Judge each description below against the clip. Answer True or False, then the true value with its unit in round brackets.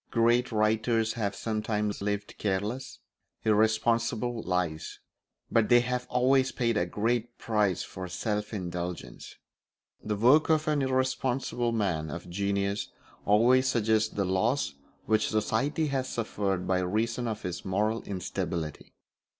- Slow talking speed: True (125 wpm)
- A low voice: True (110 Hz)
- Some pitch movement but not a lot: True (3.4 semitones)